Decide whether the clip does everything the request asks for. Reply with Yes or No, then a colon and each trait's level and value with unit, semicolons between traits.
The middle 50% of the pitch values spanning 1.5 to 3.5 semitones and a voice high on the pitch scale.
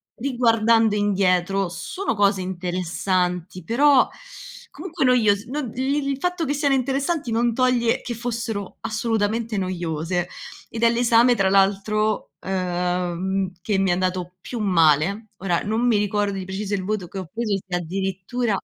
No: average, 4.2 semitones; high, 205 Hz